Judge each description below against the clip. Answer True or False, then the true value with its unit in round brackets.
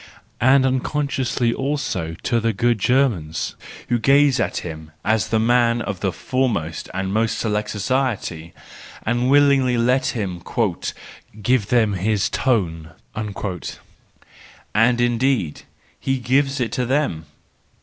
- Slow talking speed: True (125 wpm)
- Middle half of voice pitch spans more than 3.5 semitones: True (4.6 semitones)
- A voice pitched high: False (115 Hz)